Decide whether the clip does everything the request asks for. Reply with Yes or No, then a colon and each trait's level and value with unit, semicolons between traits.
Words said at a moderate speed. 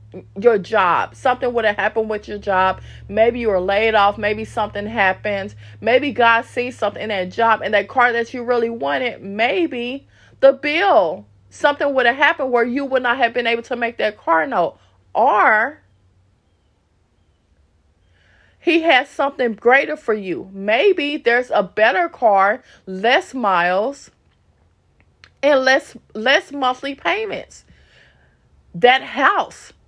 Yes: average, 145 wpm